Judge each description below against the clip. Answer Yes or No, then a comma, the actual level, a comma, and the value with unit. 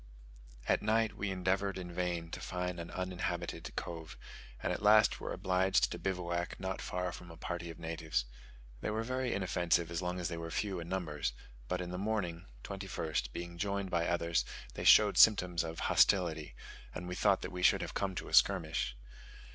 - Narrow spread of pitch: Yes, narrow, 2.3 semitones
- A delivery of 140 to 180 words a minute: No, average, 190 wpm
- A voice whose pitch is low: Yes, very low, 90 Hz